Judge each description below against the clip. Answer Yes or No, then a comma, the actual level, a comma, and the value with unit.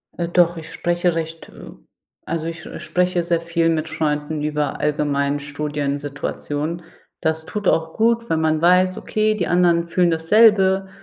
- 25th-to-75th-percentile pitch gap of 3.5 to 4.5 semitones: No, average, 2.9 semitones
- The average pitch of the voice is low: No, medium, 165 Hz